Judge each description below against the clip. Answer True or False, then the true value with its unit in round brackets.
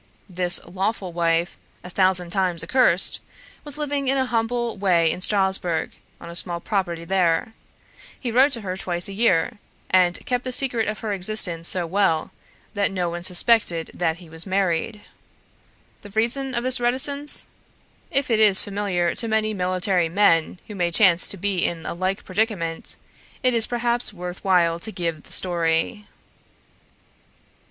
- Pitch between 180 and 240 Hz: True (190 Hz)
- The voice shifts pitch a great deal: False (4.6 semitones)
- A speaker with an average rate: True (160 wpm)